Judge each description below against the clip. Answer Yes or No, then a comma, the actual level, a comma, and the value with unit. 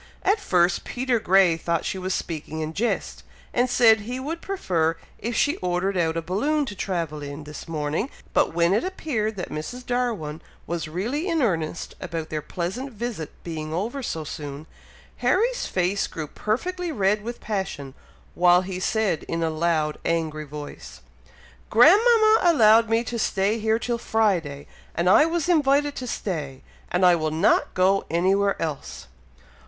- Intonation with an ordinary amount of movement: No, wide, 6.9 semitones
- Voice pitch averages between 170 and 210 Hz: Yes, high, 190 Hz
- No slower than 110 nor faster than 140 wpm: No, average, 165 wpm